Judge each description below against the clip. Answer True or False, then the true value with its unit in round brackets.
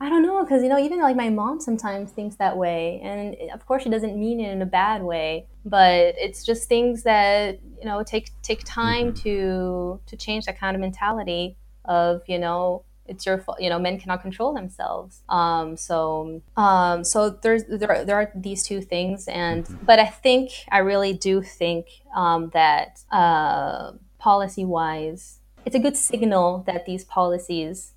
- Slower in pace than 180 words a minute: False (185 wpm)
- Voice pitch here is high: True (195 Hz)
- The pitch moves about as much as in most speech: True (3.8 semitones)